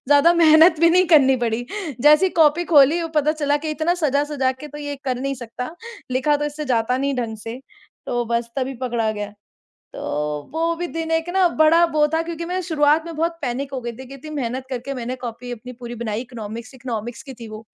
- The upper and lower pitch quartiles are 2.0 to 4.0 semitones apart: No, average, 4.4 semitones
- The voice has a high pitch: Yes, very high, 275 Hz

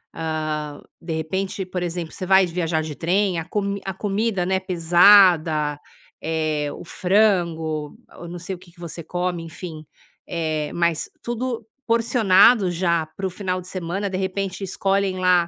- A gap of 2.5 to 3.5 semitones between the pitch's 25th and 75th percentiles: Yes, average, 2.9 semitones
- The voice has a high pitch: No, medium, 180 Hz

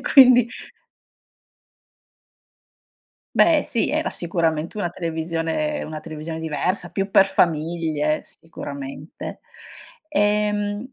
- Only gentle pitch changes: No, average, 4.8 semitones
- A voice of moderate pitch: Yes, medium, 170 Hz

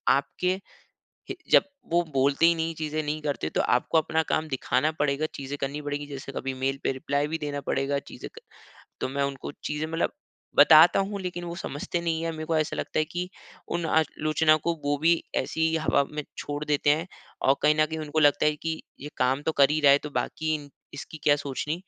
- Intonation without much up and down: Yes, narrow, 2.2 semitones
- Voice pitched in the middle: Yes, medium, 150 Hz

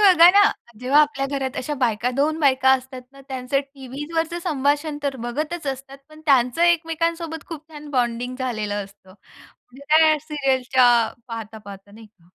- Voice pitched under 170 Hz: No, very high, 275 Hz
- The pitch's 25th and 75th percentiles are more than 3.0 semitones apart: Yes, average, 3.8 semitones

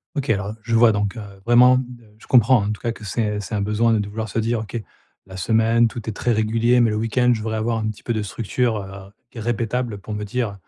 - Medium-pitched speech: No, low, 110 Hz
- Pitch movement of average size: No, narrow, 2.2 semitones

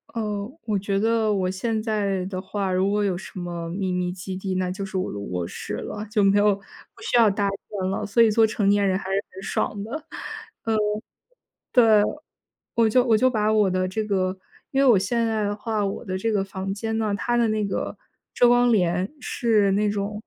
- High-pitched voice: Yes, high, 205 Hz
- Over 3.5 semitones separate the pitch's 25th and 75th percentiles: No, narrow, 2.4 semitones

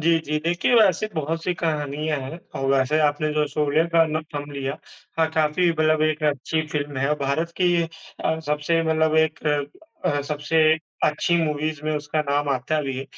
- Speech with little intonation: Yes, narrow, 1.8 semitones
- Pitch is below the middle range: No, medium, 155 Hz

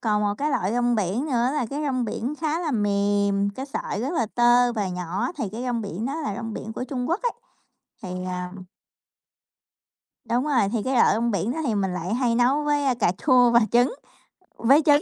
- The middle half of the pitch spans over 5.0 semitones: No, average, 4.5 semitones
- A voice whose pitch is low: No, high, 235 Hz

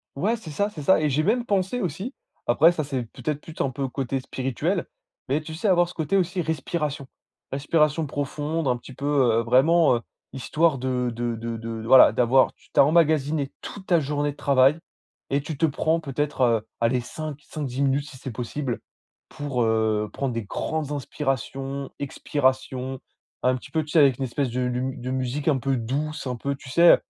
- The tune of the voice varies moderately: Yes, average, 3.4 semitones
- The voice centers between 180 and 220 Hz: No, medium, 140 Hz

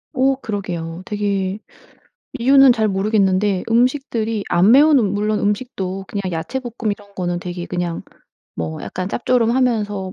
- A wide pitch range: No, average, 4.1 semitones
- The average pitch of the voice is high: Yes, high, 205 Hz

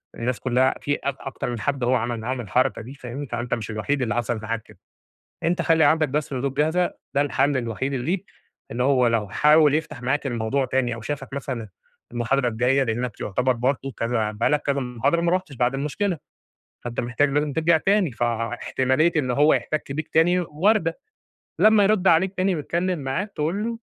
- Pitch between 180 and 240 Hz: No, low, 135 Hz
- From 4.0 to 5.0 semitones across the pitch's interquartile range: Yes, average, 4.5 semitones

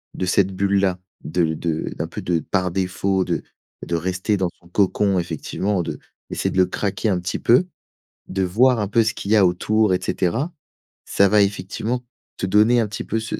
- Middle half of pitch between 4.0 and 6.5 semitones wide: No, average, 2.8 semitones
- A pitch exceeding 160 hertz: No, very low, 95 Hz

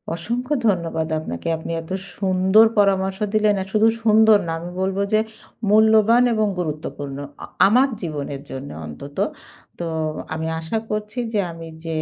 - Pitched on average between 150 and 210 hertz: Yes, high, 190 Hz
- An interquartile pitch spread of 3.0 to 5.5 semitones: Yes, average, 5.0 semitones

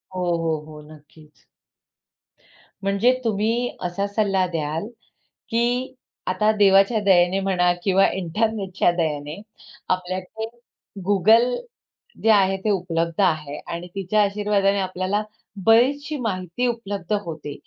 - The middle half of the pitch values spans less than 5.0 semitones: Yes, average, 3.4 semitones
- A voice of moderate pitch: No, high, 195 Hz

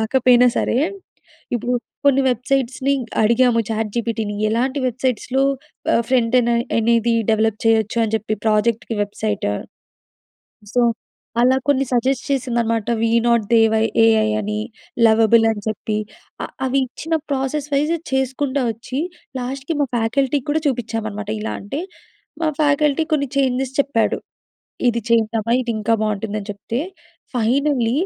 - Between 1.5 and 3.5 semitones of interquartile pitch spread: Yes, average, 3.2 semitones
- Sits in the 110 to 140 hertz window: No, high, 235 Hz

